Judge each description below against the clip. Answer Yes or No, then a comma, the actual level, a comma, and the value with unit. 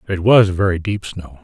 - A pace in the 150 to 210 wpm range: No, fast, 250 wpm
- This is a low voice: Yes, very low, 95 Hz